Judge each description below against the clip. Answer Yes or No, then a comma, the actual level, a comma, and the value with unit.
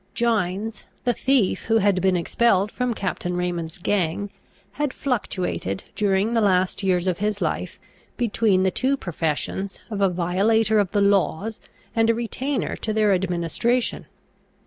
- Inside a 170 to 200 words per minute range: No, average, 145 wpm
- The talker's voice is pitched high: Yes, high, 200 Hz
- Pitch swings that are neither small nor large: Yes, average, 3.6 semitones